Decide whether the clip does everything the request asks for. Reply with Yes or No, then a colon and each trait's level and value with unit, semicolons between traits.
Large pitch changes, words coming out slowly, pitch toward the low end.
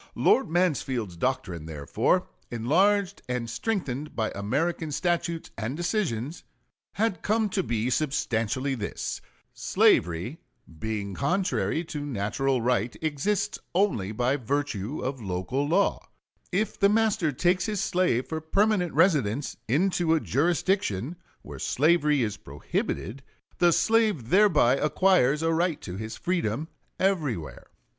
No: wide, 7.5 semitones; slow, 120 wpm; medium, 145 Hz